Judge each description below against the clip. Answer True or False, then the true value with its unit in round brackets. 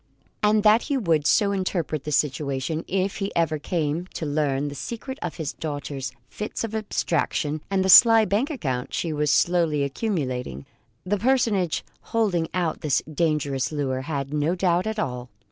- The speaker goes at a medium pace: True (165 wpm)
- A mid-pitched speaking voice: True (165 Hz)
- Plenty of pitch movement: True (5.7 semitones)